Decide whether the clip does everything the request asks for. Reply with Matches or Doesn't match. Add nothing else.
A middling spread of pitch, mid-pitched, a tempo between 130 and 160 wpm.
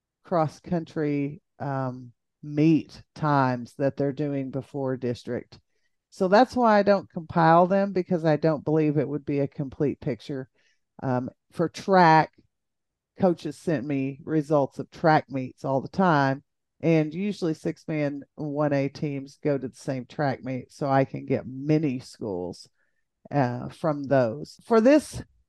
Matches